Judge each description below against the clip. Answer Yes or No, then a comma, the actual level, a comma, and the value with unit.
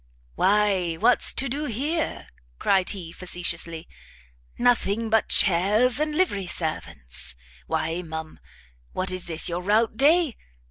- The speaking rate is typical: No, slow, 125 wpm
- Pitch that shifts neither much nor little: No, wide, 6.2 semitones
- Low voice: No, high, 195 Hz